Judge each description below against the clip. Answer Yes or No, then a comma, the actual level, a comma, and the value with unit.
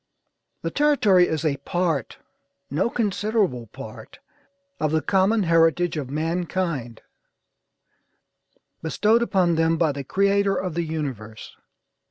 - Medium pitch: Yes, medium, 170 Hz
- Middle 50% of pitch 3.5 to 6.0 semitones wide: Yes, average, 4.4 semitones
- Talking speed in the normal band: No, slow, 115 wpm